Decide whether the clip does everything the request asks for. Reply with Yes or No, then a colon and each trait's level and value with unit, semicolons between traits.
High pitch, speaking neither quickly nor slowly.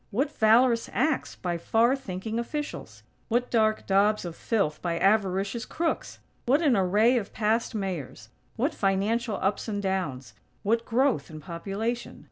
Yes: high, 215 Hz; average, 145 wpm